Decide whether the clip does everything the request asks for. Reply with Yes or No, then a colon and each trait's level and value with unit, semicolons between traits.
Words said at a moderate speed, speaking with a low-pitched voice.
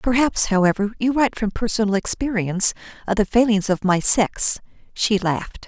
No: average, 160 wpm; high, 210 Hz